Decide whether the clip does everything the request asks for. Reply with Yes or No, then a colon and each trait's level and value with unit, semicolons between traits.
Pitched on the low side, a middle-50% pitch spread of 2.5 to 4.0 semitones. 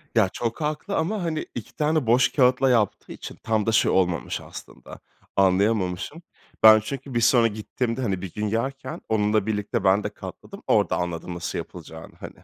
No: low, 110 Hz; average, 4.8 semitones